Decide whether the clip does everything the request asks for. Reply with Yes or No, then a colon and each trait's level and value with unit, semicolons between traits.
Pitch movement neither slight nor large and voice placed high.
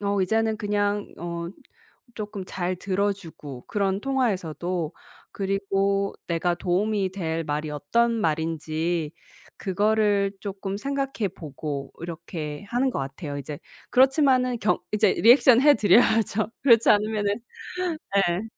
Yes: average, 4.5 semitones; high, 200 Hz